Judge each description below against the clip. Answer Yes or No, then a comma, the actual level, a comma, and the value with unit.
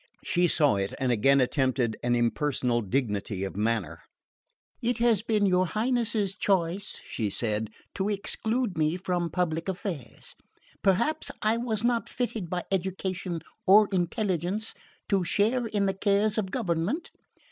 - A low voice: No, medium, 185 Hz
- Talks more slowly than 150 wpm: Yes, average, 140 wpm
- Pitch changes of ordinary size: No, wide, 7.5 semitones